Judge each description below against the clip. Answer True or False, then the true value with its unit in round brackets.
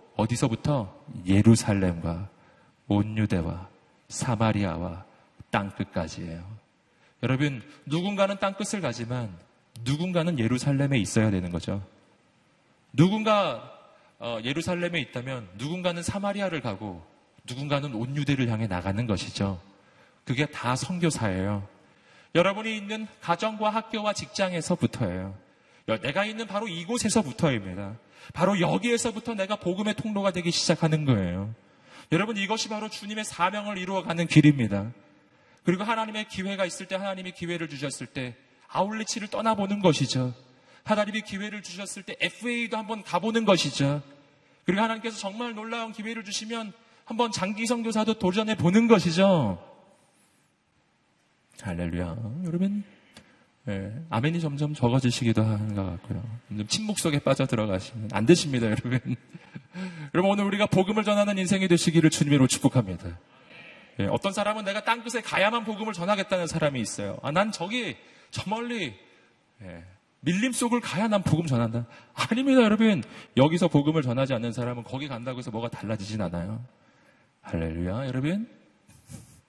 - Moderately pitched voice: True (155 Hz)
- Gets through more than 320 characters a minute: True (335 characters per minute)